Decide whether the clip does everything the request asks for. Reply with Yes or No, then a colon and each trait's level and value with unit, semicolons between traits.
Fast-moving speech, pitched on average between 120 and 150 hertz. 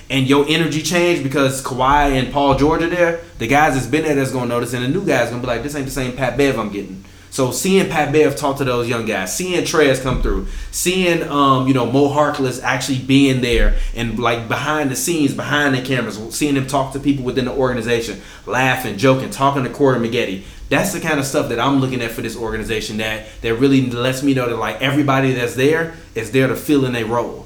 Yes: fast, 235 wpm; low, 130 Hz